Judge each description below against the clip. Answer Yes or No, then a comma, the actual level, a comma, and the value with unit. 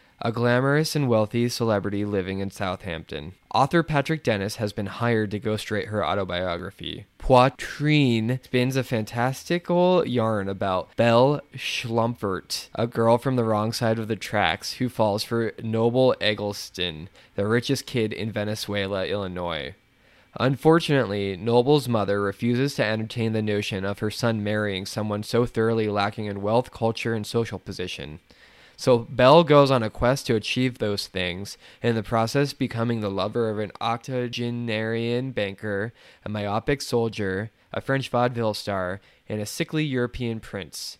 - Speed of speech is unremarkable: Yes, average, 150 wpm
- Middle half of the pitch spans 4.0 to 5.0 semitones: No, average, 3.2 semitones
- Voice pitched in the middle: No, low, 115 Hz